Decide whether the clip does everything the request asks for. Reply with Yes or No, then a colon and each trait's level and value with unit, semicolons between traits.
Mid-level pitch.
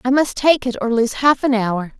No: high, 245 Hz